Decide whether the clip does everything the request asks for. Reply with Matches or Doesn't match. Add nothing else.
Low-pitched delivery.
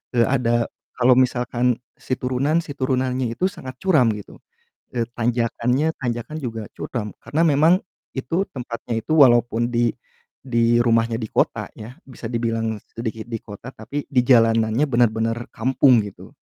Matches